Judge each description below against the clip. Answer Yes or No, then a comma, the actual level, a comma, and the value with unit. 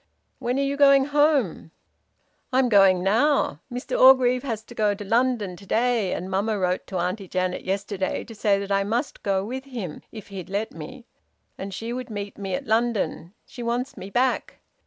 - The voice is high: Yes, high, 220 Hz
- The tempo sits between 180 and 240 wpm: Yes, average, 190 wpm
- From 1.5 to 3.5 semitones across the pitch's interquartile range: No, average, 4.4 semitones